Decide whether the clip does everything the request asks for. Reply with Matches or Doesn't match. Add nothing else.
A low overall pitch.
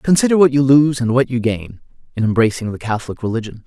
Matches